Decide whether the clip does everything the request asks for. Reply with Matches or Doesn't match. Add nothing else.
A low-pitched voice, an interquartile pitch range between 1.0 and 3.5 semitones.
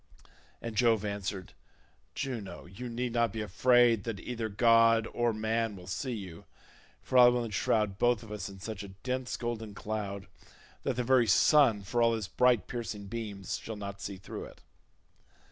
Matches